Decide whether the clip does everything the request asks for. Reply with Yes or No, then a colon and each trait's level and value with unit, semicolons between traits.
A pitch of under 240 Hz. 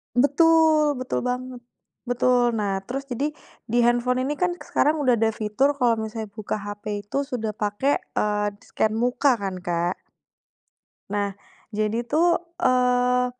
No: high, 245 Hz